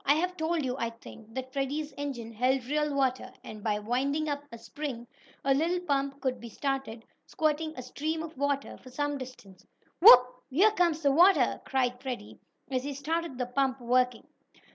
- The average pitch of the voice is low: No, very high, 270 Hz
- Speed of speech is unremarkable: Yes, average, 185 wpm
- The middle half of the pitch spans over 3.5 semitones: No, average, 3.1 semitones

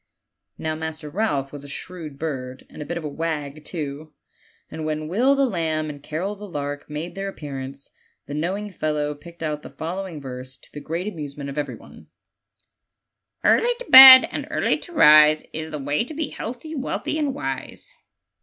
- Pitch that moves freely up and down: No, average, 4.8 semitones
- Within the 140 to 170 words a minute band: No, average, 185 wpm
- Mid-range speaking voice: Yes, medium, 155 Hz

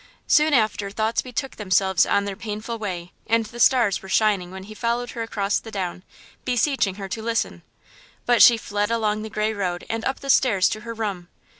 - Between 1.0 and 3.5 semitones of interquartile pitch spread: Yes, average, 2.8 semitones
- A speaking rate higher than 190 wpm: Yes, average, 200 wpm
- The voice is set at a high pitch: Yes, high, 215 Hz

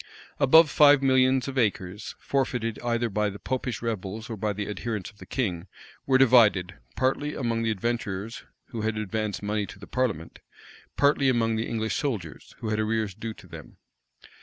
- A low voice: Yes, low, 115 Hz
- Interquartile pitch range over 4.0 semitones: No, average, 3.7 semitones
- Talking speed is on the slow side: No, average, 175 wpm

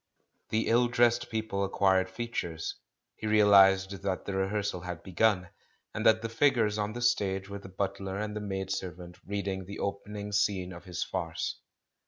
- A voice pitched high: No, low, 100 Hz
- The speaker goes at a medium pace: Yes, average, 170 wpm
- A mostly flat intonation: Yes, narrow, 2.1 semitones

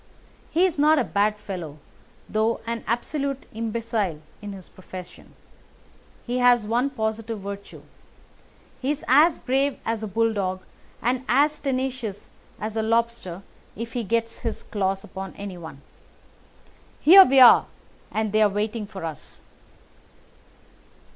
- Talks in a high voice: Yes, high, 225 Hz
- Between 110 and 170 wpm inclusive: Yes, slow, 135 wpm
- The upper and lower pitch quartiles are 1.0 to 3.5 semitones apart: No, average, 3.9 semitones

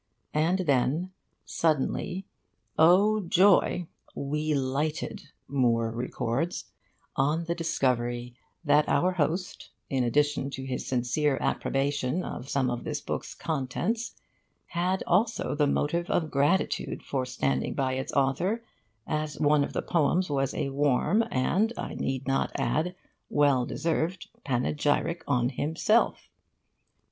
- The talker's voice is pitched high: No, medium, 145 Hz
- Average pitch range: Yes, average, 4.4 semitones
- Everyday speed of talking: No, slow, 125 wpm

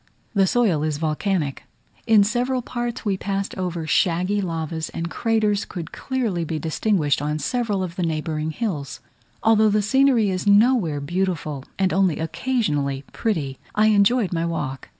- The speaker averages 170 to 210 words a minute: No, average, 150 wpm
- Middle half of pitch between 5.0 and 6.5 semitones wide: Yes, wide, 5.4 semitones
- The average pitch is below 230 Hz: Yes, medium, 185 Hz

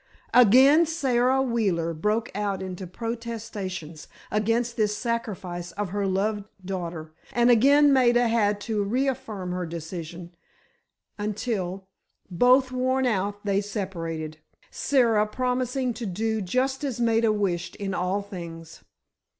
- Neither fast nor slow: No, slow, 120 wpm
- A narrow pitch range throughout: No, average, 4.6 semitones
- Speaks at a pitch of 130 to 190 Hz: No, high, 210 Hz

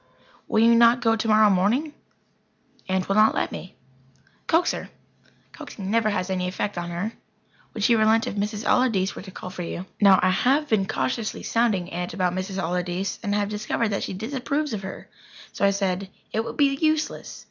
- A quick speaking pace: No, average, 195 wpm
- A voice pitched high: Yes, high, 210 Hz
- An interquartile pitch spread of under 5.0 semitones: Yes, average, 3.5 semitones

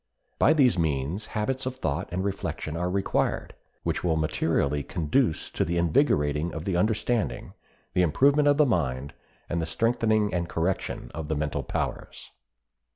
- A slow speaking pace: No, average, 155 wpm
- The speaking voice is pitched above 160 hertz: No, very low, 90 Hz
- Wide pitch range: Yes, wide, 6.1 semitones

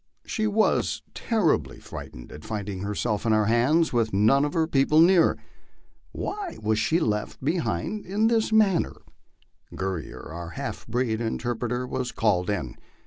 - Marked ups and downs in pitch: Yes, wide, 8.3 semitones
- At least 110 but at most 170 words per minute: Yes, average, 155 wpm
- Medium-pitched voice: No, low, 120 Hz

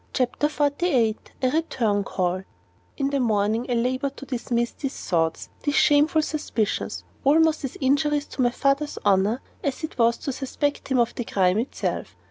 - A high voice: Yes, very high, 260 Hz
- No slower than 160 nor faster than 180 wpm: Yes, average, 165 wpm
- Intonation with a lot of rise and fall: No, average, 4.1 semitones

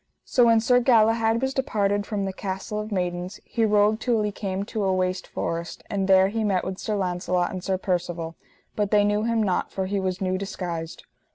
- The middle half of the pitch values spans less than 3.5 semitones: Yes, average, 2.7 semitones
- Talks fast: Yes, fast, 210 wpm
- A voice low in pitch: No, high, 200 Hz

